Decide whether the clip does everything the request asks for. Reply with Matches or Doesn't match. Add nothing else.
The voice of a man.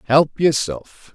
Matches